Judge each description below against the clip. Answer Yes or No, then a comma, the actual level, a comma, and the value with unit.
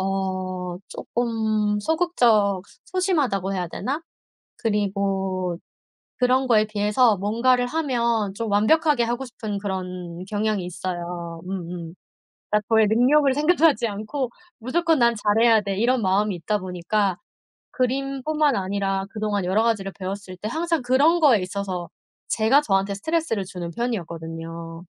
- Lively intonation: No, average, 4.8 semitones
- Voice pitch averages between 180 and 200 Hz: No, high, 210 Hz